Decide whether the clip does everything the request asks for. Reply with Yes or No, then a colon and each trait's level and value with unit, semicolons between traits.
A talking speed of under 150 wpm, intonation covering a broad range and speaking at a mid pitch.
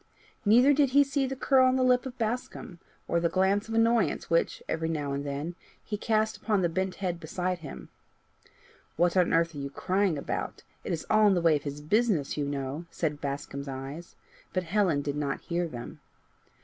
No: average, 200 wpm; wide, 6.5 semitones; medium, 175 Hz